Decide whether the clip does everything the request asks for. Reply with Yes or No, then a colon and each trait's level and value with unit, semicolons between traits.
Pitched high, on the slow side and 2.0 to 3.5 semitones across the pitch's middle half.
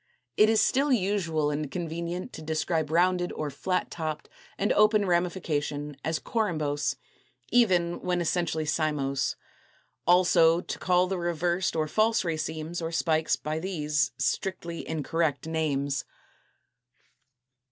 No: medium, 165 Hz; slow, 120 wpm; average, 2.8 semitones